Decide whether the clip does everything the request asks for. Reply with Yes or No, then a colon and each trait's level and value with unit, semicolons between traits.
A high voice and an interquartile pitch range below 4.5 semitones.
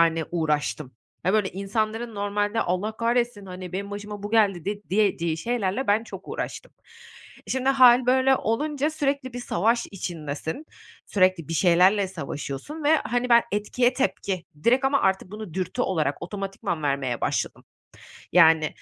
No: high, 205 Hz; average, 5.3 semitones